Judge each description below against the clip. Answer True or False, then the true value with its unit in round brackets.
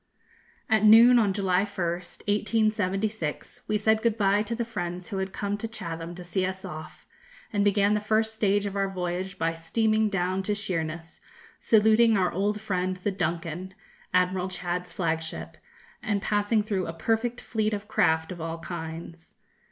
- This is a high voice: True (195 Hz)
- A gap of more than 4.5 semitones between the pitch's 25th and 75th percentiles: False (3.3 semitones)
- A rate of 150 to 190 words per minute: True (170 wpm)